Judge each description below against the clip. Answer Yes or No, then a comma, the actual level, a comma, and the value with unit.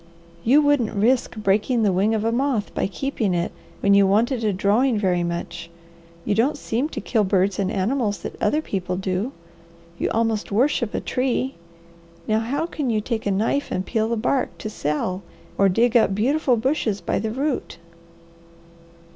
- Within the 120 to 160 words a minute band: No, average, 180 wpm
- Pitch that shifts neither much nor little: Yes, average, 4.3 semitones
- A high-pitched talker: Yes, high, 220 Hz